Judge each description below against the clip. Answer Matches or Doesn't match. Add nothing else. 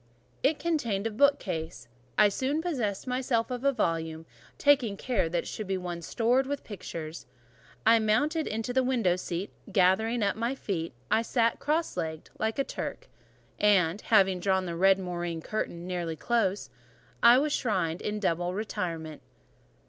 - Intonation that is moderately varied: Doesn't match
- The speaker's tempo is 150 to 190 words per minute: Matches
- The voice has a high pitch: Matches